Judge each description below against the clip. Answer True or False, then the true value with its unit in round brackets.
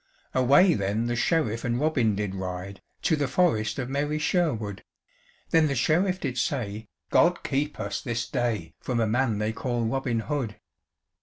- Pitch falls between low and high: False (120 Hz)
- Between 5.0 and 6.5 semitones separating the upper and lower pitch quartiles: True (5.3 semitones)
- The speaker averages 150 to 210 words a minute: True (165 wpm)